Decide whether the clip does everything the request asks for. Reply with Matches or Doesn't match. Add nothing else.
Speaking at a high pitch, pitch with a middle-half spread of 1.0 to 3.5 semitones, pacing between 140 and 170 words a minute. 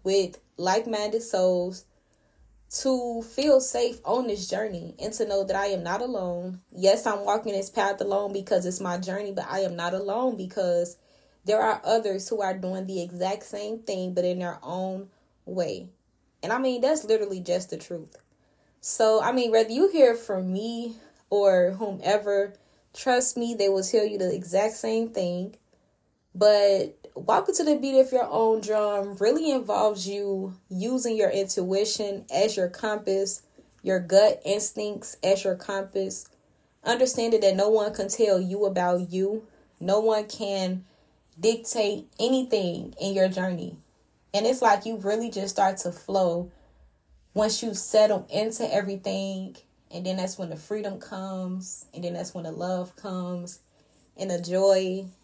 Matches